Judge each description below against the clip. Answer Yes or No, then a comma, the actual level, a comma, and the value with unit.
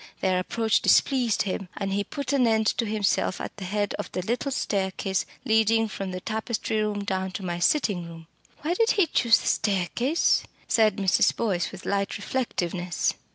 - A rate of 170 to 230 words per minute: Yes, average, 180 wpm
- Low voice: No, high, 205 Hz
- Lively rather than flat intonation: No, average, 3.3 semitones